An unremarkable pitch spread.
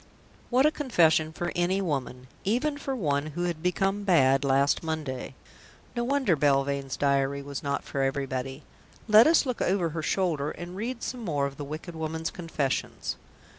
No: wide, 5.8 semitones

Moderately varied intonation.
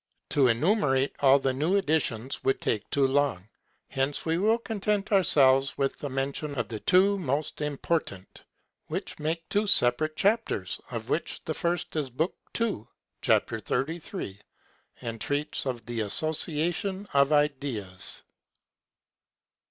Yes: average, 4.5 semitones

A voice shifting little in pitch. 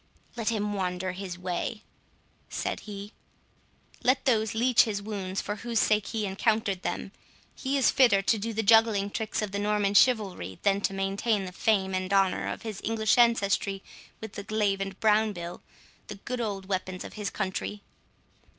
Yes: narrow, 2.2 semitones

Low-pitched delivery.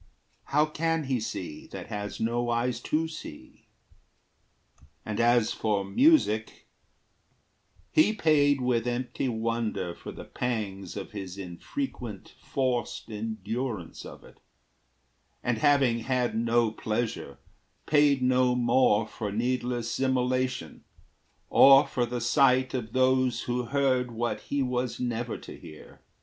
Yes: low, 120 Hz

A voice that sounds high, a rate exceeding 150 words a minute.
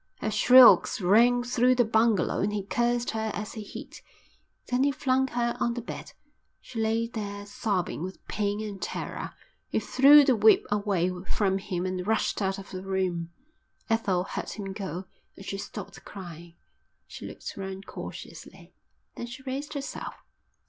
Yes: high, 210 Hz; average, 165 wpm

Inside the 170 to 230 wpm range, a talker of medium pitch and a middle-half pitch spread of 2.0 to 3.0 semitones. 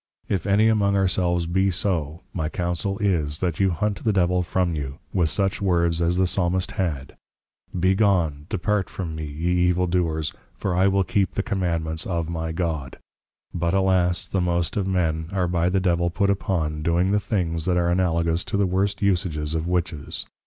No: average, 190 wpm; very low, 90 Hz; narrow, 2.6 semitones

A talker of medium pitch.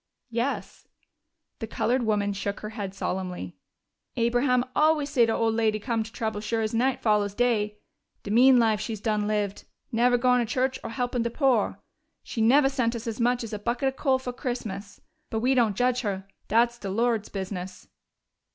No: high, 230 Hz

